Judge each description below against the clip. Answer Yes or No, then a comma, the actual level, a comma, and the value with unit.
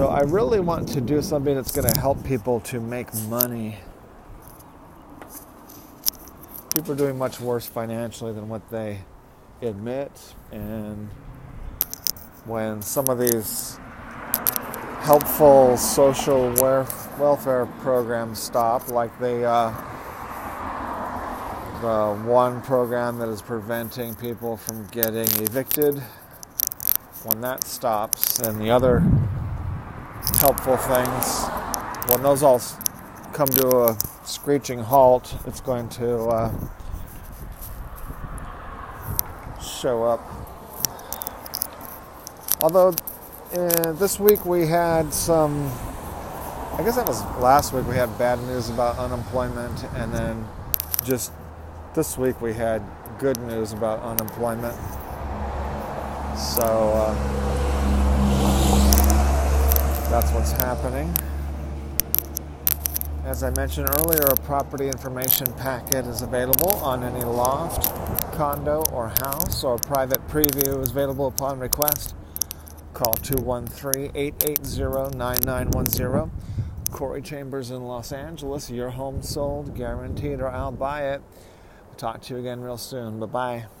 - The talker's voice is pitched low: Yes, low, 120 Hz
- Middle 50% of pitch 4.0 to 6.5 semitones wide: Yes, average, 4.6 semitones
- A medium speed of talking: No, slow, 110 wpm